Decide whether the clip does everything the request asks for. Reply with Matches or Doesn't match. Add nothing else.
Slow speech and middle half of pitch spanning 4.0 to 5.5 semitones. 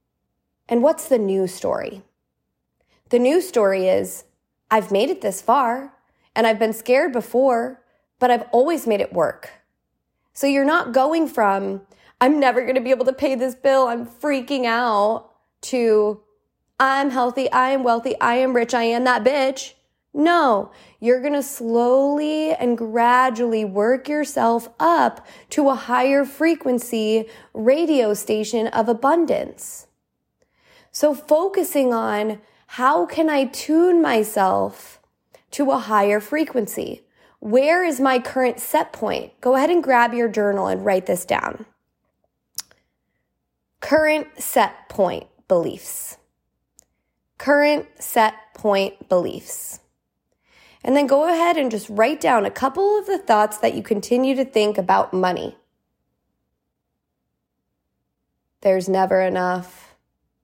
Matches